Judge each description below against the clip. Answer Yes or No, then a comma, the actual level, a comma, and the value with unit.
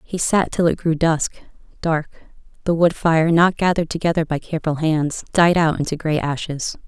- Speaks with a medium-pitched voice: Yes, medium, 160 Hz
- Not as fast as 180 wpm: No, average, 185 wpm